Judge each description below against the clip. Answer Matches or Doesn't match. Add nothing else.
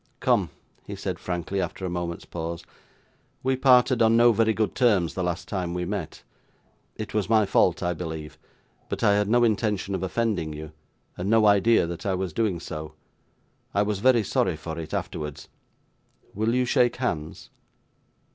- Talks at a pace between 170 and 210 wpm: Matches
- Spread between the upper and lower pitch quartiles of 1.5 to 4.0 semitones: Doesn't match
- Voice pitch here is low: Matches